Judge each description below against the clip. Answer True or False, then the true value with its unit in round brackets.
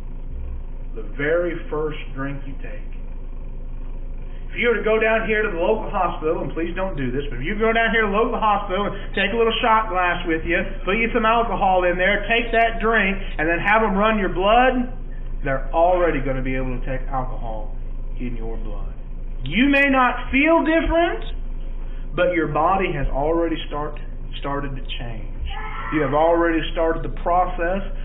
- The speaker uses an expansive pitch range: True (8.5 semitones)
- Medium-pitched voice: True (170 Hz)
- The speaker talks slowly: False (190 wpm)